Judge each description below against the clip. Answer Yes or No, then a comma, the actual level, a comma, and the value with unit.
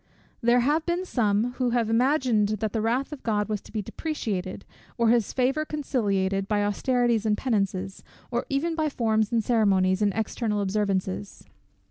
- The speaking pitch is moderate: No, high, 225 Hz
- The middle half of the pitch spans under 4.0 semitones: Yes, average, 3.6 semitones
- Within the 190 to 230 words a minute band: No, average, 165 wpm